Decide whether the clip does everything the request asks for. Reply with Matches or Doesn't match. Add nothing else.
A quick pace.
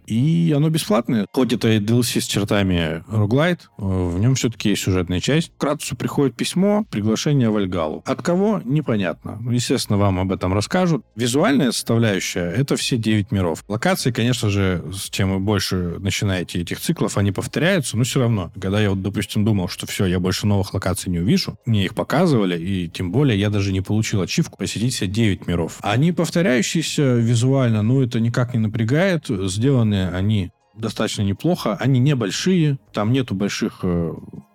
Matches